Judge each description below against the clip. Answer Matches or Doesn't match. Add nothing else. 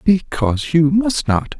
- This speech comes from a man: Matches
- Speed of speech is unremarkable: Matches